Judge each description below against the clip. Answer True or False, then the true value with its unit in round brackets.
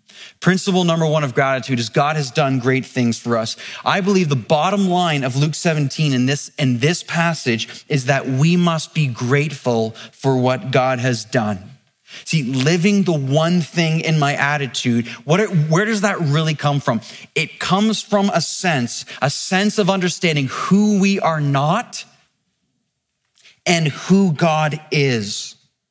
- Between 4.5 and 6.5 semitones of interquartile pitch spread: True (4.8 semitones)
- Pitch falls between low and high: True (150 Hz)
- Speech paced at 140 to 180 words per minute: True (160 wpm)